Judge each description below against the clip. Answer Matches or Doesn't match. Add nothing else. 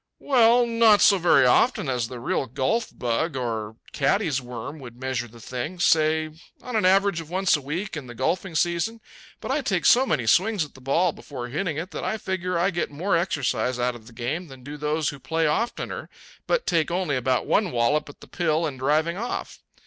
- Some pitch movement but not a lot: Doesn't match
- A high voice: Doesn't match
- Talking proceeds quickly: Matches